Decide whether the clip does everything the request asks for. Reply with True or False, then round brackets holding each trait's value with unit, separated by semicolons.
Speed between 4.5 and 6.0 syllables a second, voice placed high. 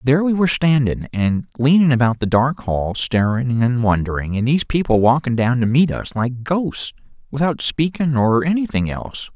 False (5.1 syllables/s; 130 Hz)